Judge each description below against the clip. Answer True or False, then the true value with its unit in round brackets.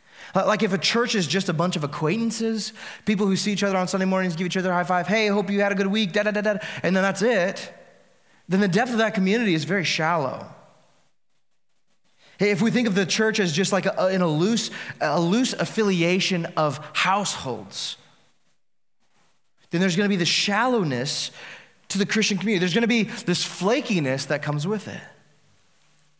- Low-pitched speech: False (195 Hz)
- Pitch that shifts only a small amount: False (3.2 semitones)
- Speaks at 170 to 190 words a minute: False (200 wpm)